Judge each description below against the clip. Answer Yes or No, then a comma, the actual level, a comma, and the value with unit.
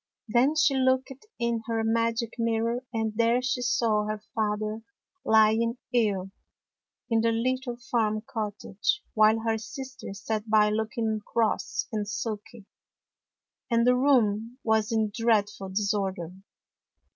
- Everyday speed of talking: No, slow, 125 wpm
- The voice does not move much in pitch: Yes, narrow, 1.9 semitones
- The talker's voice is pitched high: Yes, high, 225 Hz